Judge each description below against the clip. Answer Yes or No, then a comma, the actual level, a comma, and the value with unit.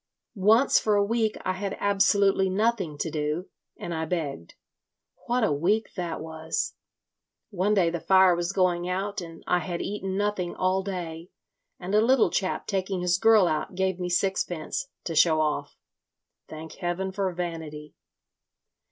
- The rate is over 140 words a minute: Yes, average, 155 wpm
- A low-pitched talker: No, medium, 185 Hz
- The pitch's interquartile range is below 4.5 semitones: Yes, average, 3.1 semitones